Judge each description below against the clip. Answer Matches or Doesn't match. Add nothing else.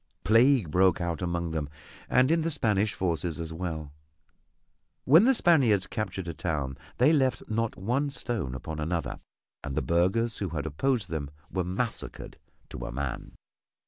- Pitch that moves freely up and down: Matches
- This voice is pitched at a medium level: Doesn't match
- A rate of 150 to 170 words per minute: Matches